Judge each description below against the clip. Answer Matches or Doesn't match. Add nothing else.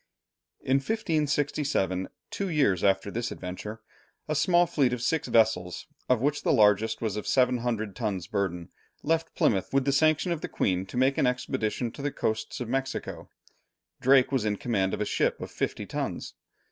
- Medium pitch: Doesn't match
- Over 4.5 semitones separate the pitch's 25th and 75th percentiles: Matches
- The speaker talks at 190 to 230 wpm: Doesn't match